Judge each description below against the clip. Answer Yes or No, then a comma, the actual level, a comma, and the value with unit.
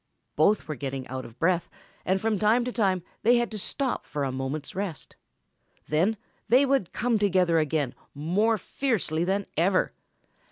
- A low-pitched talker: No, medium, 185 Hz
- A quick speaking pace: No, average, 165 wpm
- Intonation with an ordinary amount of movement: No, wide, 6.3 semitones